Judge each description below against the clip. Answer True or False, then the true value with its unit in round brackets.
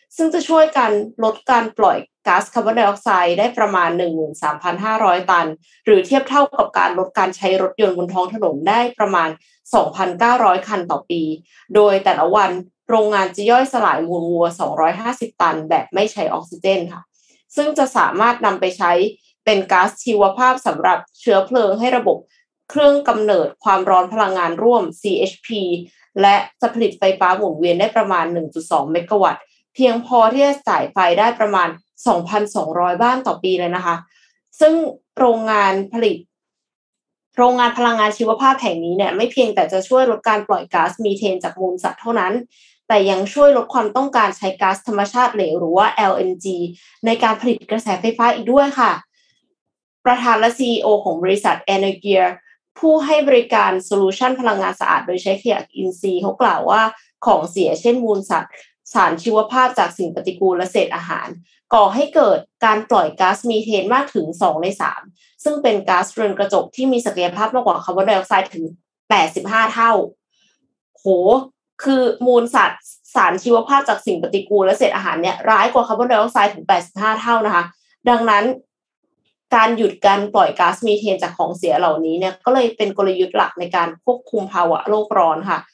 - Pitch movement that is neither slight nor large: True (4.4 semitones)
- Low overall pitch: False (210 Hz)